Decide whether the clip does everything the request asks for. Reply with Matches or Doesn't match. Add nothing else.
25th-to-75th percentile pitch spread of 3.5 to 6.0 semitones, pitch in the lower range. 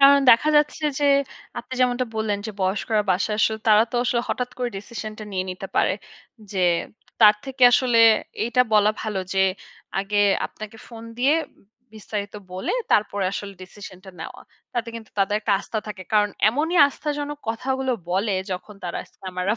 Doesn't match